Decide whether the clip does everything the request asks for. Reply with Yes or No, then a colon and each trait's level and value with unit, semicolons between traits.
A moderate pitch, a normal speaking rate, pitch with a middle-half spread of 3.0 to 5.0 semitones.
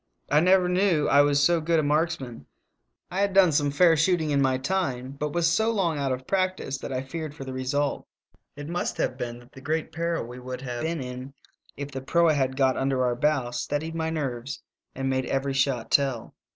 No: medium, 145 Hz; fast, 215 wpm; average, 3.9 semitones